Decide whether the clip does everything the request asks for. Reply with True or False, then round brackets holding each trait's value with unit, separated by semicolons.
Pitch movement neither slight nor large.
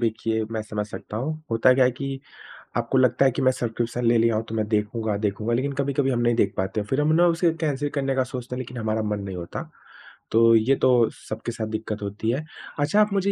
True (3.5 semitones)